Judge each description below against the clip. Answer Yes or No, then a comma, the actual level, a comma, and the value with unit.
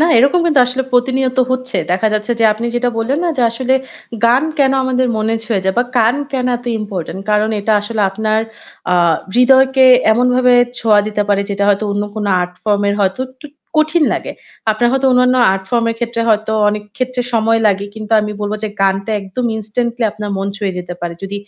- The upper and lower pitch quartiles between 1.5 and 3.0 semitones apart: No, average, 3.5 semitones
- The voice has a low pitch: No, high, 225 Hz